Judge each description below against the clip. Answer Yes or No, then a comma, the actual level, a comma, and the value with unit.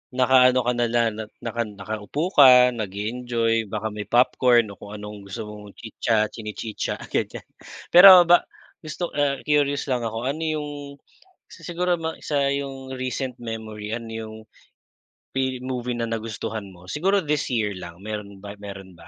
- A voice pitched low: Yes, low, 120 Hz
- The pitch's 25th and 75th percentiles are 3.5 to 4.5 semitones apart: Yes, average, 4.1 semitones